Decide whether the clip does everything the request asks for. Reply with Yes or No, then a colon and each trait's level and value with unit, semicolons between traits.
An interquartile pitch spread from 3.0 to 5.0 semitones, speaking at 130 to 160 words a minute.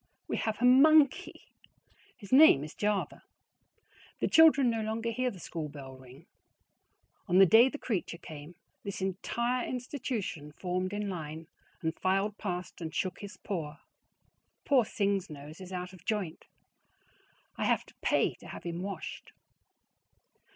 No: wide, 5.4 semitones; average, 150 wpm